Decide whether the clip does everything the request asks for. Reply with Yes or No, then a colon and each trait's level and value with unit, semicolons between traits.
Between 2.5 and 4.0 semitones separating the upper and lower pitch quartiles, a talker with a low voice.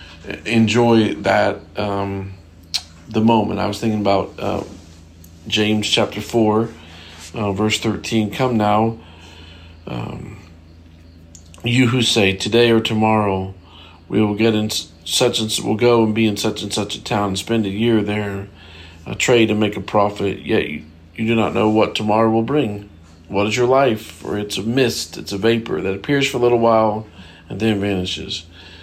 No: average, 4.7 semitones; low, 105 Hz